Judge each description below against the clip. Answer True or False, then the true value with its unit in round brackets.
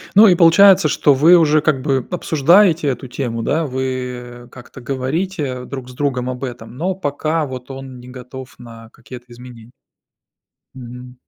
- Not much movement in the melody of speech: False (3.6 semitones)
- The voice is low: True (130 Hz)